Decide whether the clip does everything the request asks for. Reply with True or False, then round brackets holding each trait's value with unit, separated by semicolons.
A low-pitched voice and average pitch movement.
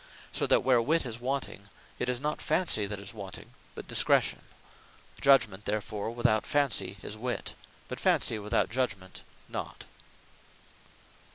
True (115 Hz; 3.9 semitones)